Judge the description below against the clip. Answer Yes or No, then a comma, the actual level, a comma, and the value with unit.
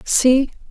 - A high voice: Yes, very high, 260 Hz